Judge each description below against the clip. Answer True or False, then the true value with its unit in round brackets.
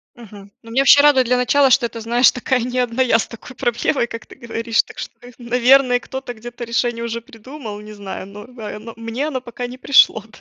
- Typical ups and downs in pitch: False (1.9 semitones)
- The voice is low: False (240 Hz)